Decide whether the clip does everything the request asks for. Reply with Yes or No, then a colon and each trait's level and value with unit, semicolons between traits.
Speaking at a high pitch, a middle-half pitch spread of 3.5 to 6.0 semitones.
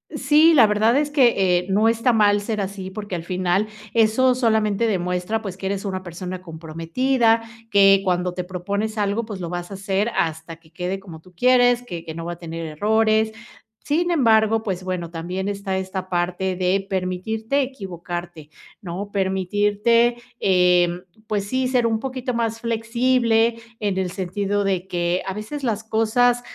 Yes: high, 200 Hz; average, 3.8 semitones